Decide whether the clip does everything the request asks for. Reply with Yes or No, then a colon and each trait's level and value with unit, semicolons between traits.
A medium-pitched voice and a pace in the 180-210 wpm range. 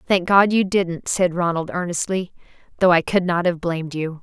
Yes: medium, 175 Hz; average, 200 wpm